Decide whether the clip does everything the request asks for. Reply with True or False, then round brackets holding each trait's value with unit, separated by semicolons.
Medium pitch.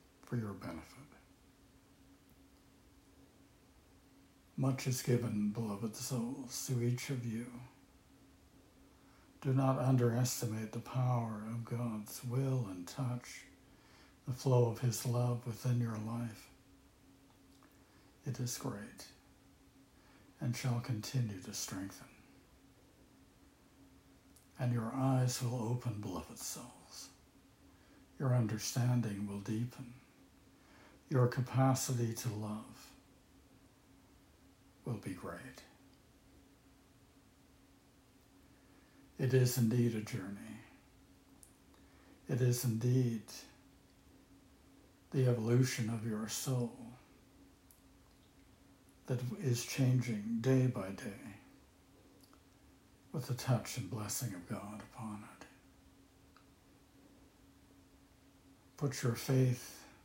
False (120 Hz)